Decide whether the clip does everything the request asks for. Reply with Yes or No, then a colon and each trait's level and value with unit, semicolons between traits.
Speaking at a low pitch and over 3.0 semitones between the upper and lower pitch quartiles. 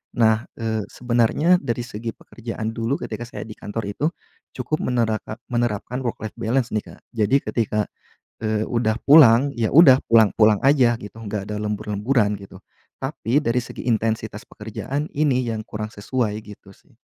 No: low, 115 Hz; narrow, 2.5 semitones